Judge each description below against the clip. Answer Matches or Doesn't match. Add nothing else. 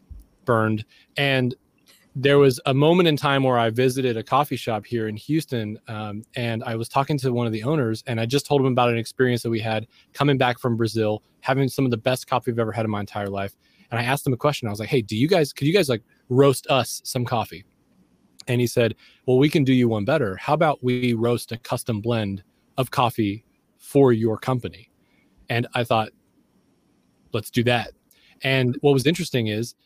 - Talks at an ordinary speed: Doesn't match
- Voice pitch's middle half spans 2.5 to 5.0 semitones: Matches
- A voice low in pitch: Matches